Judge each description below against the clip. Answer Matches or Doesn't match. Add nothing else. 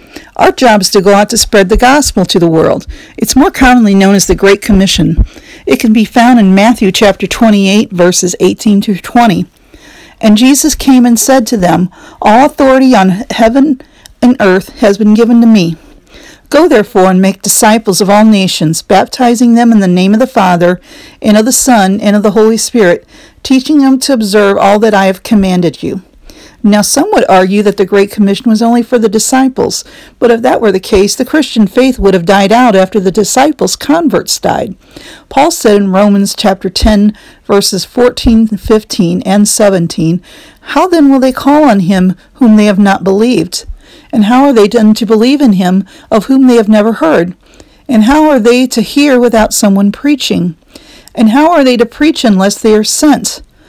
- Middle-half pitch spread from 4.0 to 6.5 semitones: Matches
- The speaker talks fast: Doesn't match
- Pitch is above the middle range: Matches